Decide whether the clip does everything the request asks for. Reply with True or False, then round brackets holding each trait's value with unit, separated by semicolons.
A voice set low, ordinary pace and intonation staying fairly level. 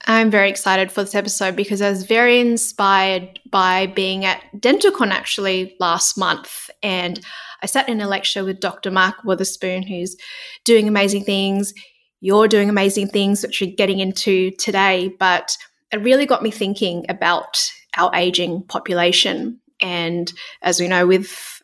False (195 Hz; 155 wpm; 2.2 semitones)